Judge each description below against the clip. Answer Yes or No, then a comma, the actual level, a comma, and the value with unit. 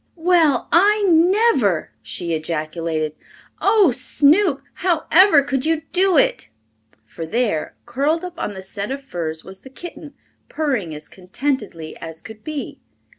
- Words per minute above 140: No, slow, 135 wpm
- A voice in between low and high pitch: No, very high, 265 Hz